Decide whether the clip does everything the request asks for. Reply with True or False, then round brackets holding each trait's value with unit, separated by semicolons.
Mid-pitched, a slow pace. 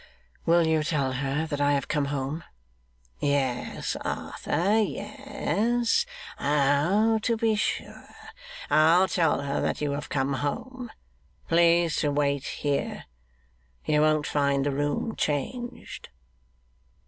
True (150 Hz; 120 wpm)